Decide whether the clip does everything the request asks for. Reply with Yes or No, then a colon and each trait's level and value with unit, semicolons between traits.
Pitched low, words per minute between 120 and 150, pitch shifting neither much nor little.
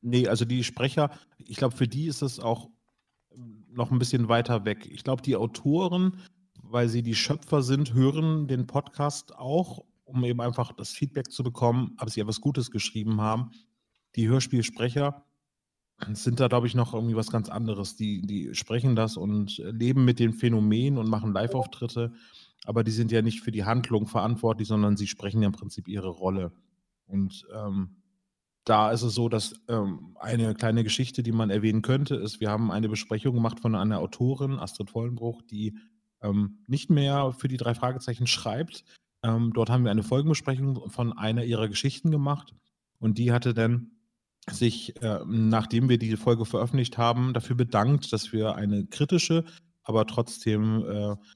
No: low, 120 Hz; average, 175 wpm; average, 3.2 semitones